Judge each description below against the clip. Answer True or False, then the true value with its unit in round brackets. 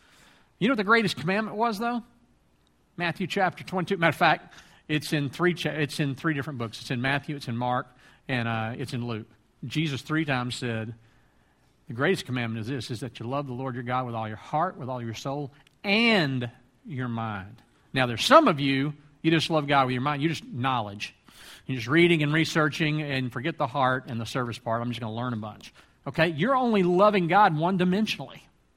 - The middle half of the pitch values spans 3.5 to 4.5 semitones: False (5.2 semitones)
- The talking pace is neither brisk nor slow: False (220 wpm)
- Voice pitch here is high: False (140 Hz)